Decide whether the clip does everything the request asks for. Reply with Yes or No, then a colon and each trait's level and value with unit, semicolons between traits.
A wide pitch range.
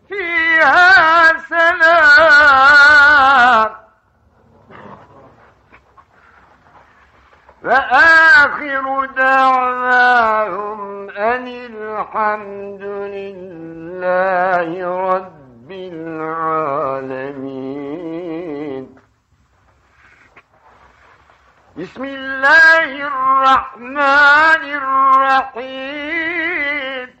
Yes: wide, 7.9 semitones